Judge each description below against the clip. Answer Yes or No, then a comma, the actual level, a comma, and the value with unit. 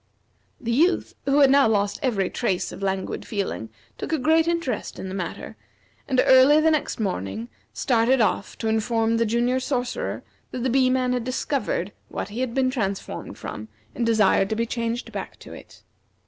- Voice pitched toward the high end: Yes, high, 235 Hz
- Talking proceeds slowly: No, average, 185 wpm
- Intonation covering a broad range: No, average, 3.9 semitones